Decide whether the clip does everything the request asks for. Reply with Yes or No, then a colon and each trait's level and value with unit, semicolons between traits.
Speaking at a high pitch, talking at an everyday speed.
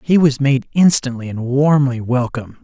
No: low, 135 Hz; average, 160 wpm